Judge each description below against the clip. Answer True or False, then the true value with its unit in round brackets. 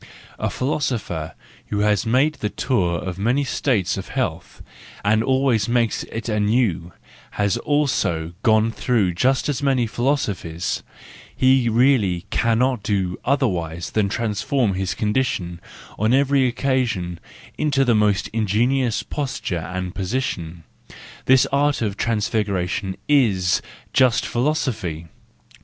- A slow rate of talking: True (115 wpm)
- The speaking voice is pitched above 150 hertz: False (110 Hz)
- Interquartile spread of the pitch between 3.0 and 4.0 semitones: False (5.6 semitones)